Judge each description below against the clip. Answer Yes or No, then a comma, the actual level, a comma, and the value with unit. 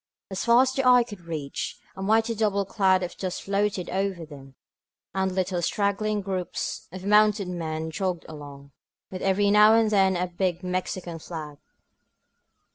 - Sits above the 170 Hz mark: Yes, high, 190 Hz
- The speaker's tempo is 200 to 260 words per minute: No, average, 160 wpm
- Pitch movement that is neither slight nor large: Yes, average, 3.1 semitones